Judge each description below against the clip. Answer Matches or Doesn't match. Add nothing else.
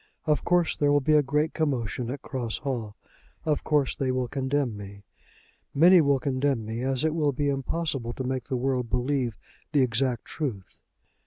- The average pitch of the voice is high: Doesn't match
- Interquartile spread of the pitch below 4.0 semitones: Matches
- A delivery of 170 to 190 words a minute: Matches